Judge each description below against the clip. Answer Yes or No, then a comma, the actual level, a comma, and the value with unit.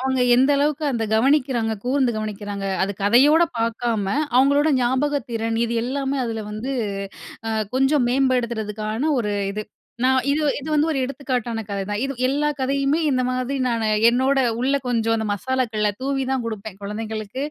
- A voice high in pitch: Yes, very high, 250 Hz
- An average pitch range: Yes, average, 3.6 semitones